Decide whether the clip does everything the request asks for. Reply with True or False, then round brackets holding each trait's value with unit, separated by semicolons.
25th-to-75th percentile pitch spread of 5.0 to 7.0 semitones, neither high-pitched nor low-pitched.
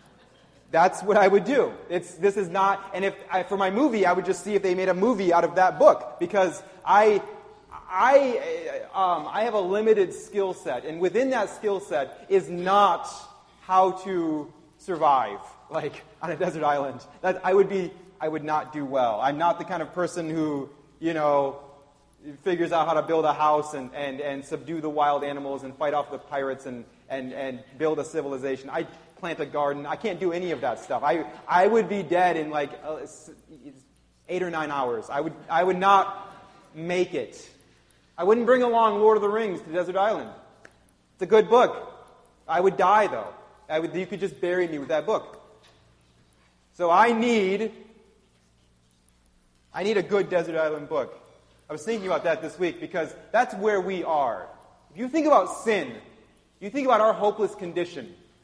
True (5.6 semitones; 180 Hz)